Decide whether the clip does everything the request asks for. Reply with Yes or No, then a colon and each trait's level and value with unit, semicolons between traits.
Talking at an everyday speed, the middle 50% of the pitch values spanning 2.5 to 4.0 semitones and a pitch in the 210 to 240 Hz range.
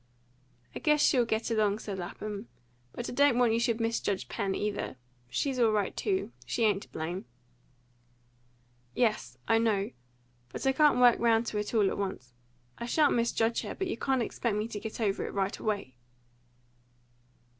Yes: average, 175 wpm; average, 2.8 semitones; high, 225 Hz